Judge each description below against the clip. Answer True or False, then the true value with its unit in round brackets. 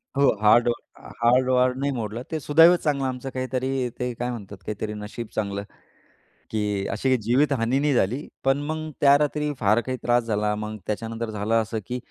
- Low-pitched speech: True (125 Hz)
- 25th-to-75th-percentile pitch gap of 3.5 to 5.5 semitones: True (3.8 semitones)